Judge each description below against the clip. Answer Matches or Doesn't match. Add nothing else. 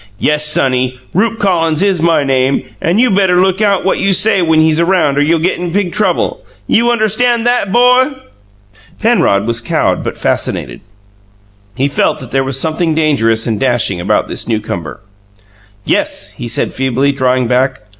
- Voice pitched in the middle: Matches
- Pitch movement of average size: Doesn't match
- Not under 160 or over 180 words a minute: Matches